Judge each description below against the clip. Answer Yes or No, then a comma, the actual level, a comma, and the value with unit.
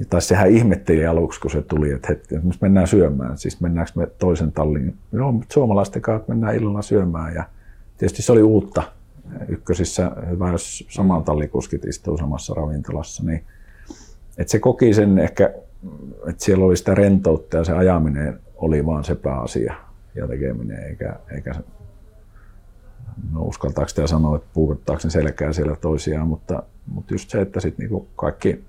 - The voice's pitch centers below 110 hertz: Yes, very low, 90 Hz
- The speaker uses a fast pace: Yes, fast, 160 wpm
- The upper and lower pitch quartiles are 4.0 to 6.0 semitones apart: Yes, average, 4.5 semitones